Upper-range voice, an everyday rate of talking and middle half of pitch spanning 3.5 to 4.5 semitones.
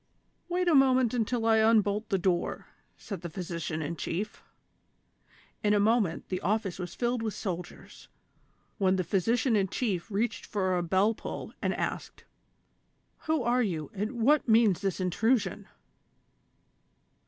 Yes: high, 210 Hz; average, 150 wpm; average, 4.0 semitones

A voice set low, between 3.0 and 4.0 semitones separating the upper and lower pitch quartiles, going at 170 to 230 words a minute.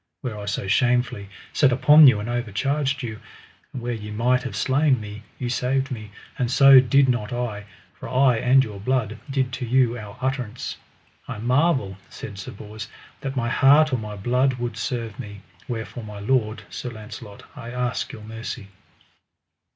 Yes: low, 120 Hz; average, 3.5 semitones; average, 175 wpm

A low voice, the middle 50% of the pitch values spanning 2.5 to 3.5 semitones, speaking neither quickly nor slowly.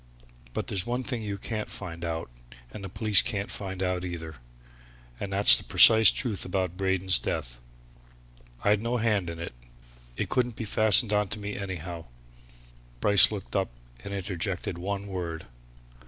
Yes: low, 100 Hz; average, 2.8 semitones; average, 160 wpm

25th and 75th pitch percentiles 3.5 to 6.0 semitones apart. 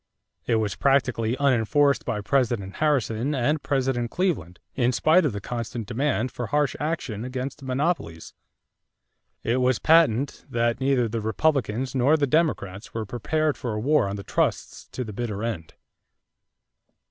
Yes: average, 4.2 semitones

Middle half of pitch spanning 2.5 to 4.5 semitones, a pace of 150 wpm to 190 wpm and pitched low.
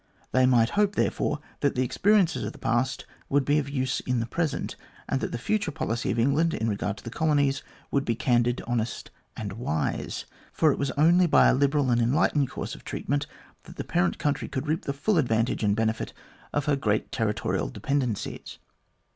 No: average, 4.1 semitones; average, 200 wpm; low, 130 Hz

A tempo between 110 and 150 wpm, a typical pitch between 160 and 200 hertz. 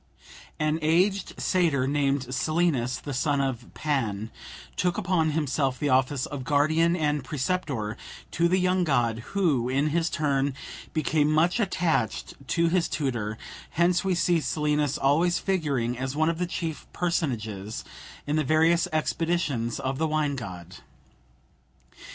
No: average, 145 wpm; medium, 150 Hz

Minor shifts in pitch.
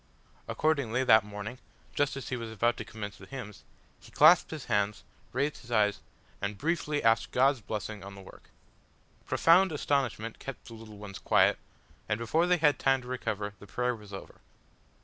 No: average, 4.6 semitones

